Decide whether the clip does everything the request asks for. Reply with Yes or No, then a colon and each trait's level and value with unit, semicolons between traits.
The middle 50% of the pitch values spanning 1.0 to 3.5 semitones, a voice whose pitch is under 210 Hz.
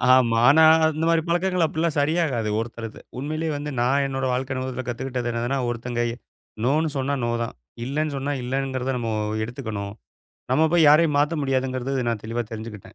No: average, 4.0 semitones; low, 135 Hz